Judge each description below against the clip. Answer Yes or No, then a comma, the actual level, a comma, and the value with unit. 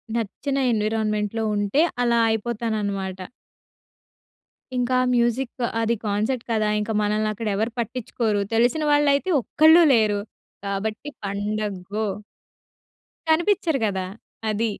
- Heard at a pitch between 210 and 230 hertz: Yes, high, 220 Hz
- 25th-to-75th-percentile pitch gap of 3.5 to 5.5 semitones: No, average, 2.8 semitones